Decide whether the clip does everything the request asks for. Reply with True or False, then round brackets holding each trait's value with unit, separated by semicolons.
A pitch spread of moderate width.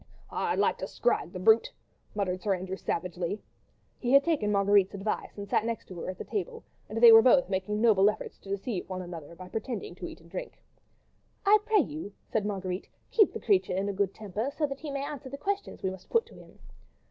False (6.8 semitones)